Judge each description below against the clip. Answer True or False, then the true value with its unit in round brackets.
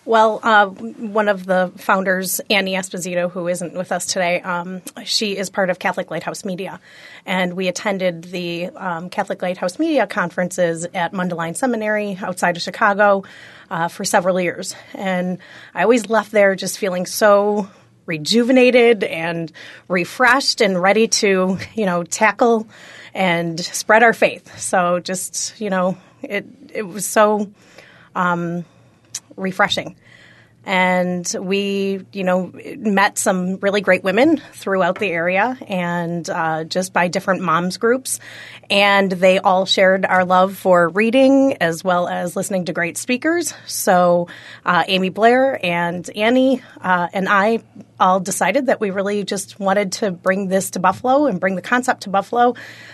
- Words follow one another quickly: False (150 wpm)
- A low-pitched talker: False (190 Hz)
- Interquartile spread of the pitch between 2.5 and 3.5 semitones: True (2.9 semitones)